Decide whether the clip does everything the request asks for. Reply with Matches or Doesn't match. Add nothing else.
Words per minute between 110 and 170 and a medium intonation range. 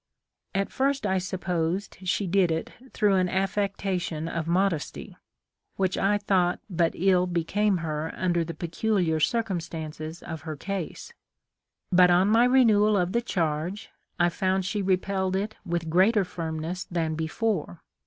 Matches